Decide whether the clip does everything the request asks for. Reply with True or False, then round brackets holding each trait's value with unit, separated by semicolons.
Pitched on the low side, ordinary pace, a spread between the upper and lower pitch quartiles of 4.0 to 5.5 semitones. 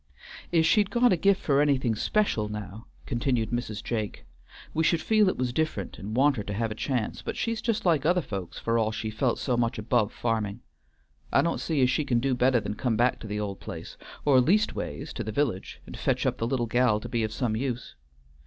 False (120 Hz; 225 wpm; 5.1 semitones)